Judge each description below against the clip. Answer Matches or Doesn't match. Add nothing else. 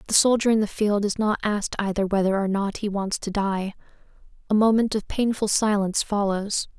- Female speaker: Matches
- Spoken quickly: Doesn't match